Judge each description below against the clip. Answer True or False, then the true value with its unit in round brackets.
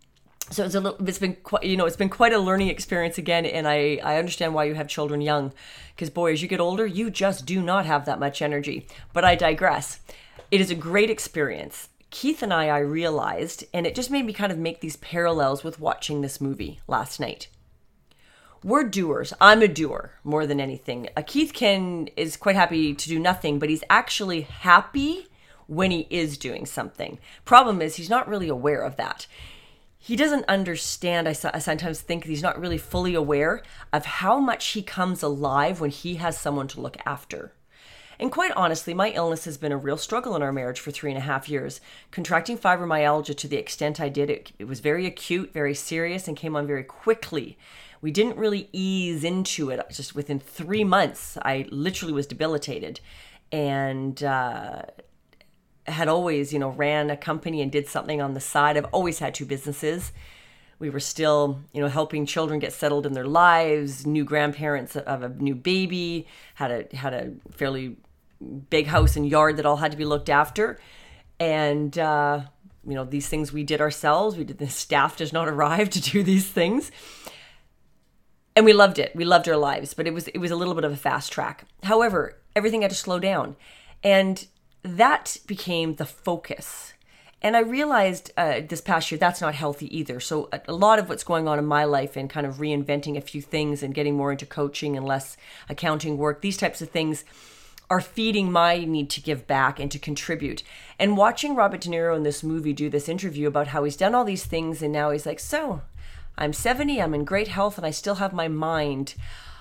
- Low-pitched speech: False (160 Hz)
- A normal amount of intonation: True (3.9 semitones)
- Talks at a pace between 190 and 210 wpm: True (200 wpm)